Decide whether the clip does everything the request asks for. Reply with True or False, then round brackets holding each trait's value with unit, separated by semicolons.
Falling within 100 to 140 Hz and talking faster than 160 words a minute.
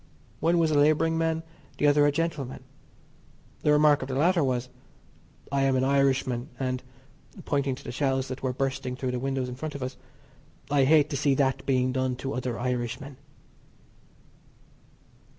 True (135 Hz; 170 wpm)